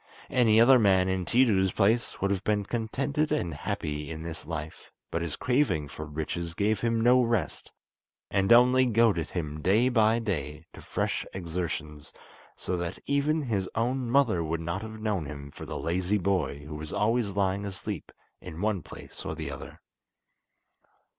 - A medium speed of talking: Yes, average, 170 wpm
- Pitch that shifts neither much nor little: No, wide, 5.8 semitones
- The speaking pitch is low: Yes, low, 100 Hz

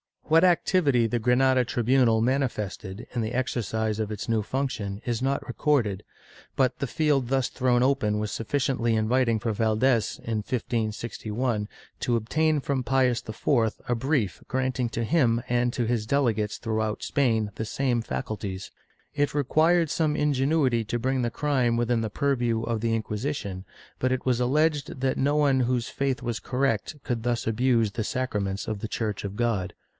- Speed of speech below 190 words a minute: Yes, average, 170 wpm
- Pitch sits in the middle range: No, low, 120 Hz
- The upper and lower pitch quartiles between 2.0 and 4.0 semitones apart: Yes, average, 3.3 semitones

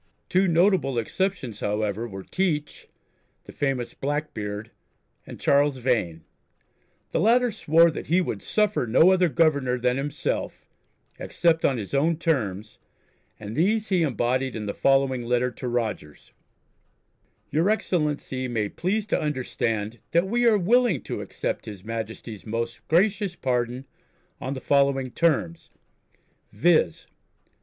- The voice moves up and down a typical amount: No, wide, 6.6 semitones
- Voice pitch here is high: No, low, 135 Hz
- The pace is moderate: No, slow, 130 wpm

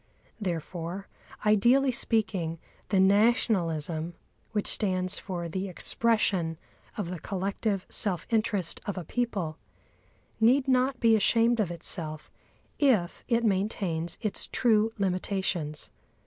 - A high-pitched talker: Yes, high, 195 Hz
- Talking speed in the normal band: No, slow, 110 wpm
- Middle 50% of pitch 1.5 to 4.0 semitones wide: No, average, 4.5 semitones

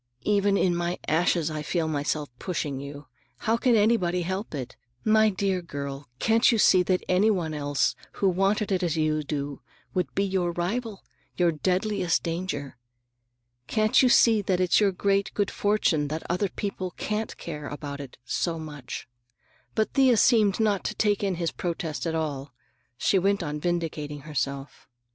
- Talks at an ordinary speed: Yes, average, 165 wpm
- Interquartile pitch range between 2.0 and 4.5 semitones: No, average, 4.9 semitones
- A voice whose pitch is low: No, medium, 180 Hz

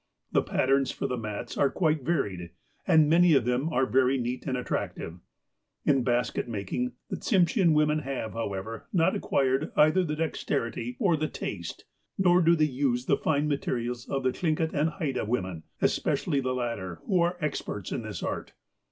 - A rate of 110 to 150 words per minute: No, average, 180 wpm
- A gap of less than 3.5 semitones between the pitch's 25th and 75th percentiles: No, average, 4.4 semitones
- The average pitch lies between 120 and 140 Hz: Yes, low, 135 Hz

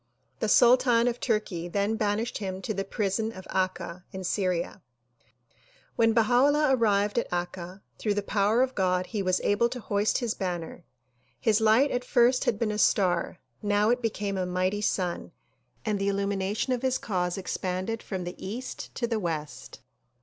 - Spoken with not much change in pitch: No, average, 3.7 semitones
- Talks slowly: No, average, 175 wpm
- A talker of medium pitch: No, high, 205 Hz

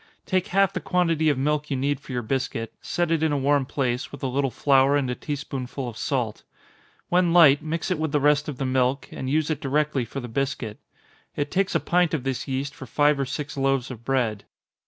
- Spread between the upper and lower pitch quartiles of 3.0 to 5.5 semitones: No, narrow, 2.6 semitones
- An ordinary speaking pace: No, fast, 235 wpm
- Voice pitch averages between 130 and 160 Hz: Yes, medium, 140 Hz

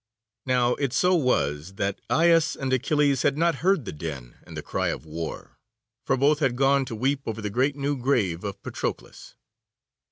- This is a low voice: Yes, low, 130 Hz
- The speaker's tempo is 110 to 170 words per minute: No, average, 185 wpm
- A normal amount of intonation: No, wide, 6.3 semitones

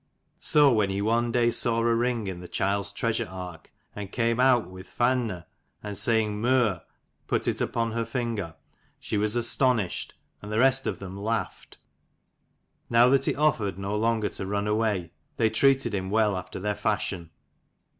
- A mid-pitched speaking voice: No, low, 110 Hz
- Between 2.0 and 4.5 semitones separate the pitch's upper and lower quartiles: Yes, average, 3.1 semitones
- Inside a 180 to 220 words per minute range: No, average, 170 wpm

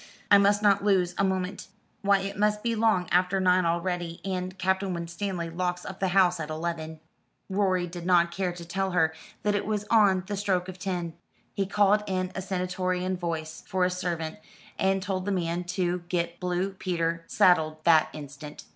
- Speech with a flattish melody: Yes, narrow, 2.1 semitones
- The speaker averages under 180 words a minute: No, average, 185 wpm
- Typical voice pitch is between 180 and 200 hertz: Yes, medium, 185 Hz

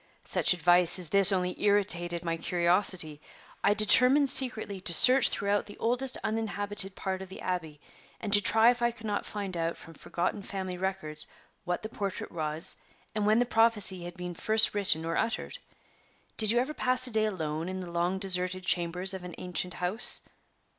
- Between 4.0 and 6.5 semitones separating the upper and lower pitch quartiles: No, average, 3.5 semitones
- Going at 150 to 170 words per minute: No, average, 185 wpm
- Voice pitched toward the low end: No, high, 190 Hz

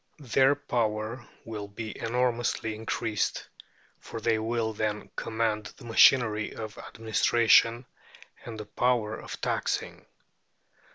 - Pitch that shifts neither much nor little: No, narrow, 1.7 semitones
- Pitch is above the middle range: No, low, 115 Hz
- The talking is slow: Yes, slow, 110 wpm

